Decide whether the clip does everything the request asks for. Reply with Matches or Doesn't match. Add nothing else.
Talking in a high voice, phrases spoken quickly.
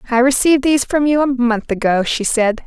Matches